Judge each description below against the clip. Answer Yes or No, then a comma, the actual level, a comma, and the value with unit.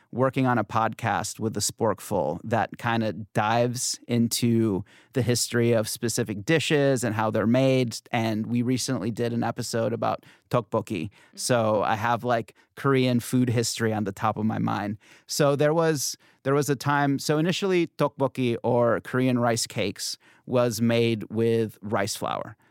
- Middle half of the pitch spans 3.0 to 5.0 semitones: No, narrow, 2.6 semitones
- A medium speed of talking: Yes, average, 160 wpm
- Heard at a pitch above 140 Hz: No, low, 120 Hz